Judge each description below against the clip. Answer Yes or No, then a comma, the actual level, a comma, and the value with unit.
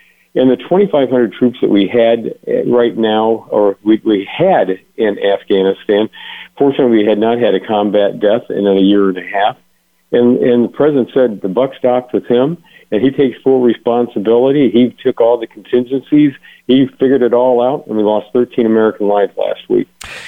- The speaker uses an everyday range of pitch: Yes, average, 3.2 semitones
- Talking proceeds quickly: No, average, 185 wpm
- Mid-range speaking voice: No, low, 120 Hz